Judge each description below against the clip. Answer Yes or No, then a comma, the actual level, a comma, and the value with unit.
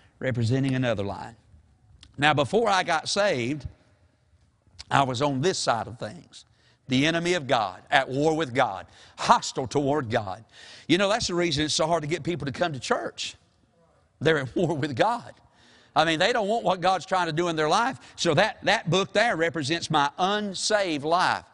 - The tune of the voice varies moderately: No, wide, 6.3 semitones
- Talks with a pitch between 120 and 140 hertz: No, medium, 150 Hz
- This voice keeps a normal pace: Yes, average, 190 wpm